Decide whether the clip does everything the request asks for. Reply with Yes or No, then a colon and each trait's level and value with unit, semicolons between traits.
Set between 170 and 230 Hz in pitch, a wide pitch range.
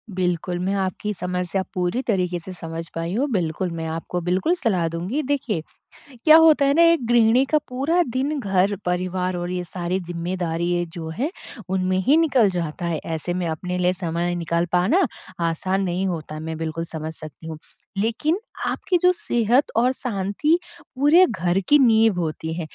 Yes: medium, 185 Hz; wide, 5.8 semitones